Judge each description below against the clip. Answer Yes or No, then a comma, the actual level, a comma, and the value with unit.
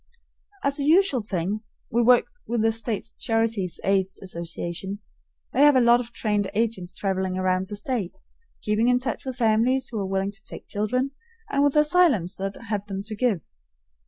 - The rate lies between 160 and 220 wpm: Yes, average, 180 wpm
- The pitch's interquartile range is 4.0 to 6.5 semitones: Yes, average, 4.3 semitones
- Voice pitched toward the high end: Yes, high, 220 Hz